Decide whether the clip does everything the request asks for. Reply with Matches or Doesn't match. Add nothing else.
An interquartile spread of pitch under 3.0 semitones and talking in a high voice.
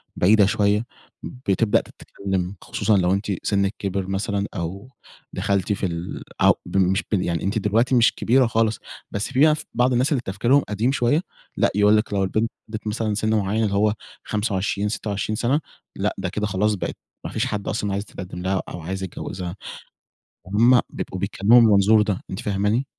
Doesn't match